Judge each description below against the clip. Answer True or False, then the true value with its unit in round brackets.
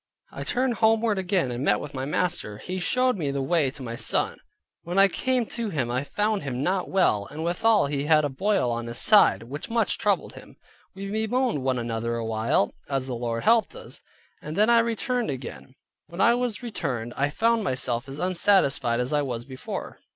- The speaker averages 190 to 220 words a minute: True (205 wpm)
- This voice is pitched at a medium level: True (150 Hz)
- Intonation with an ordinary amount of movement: False (8.9 semitones)